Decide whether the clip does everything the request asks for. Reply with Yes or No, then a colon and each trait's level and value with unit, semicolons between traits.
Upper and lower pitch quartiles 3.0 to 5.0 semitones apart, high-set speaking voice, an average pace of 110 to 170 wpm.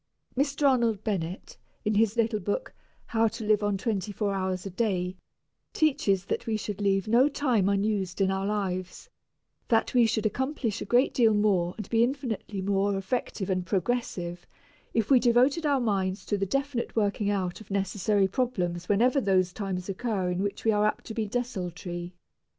No: average, 3.5 semitones; high, 205 Hz; average, 180 wpm